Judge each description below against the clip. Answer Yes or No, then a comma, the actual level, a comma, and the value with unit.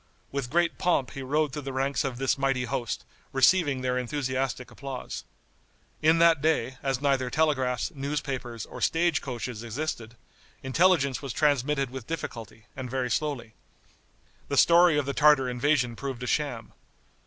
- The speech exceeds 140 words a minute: Yes, average, 155 wpm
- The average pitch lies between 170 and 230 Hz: No, low, 135 Hz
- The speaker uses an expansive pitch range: No, average, 2.9 semitones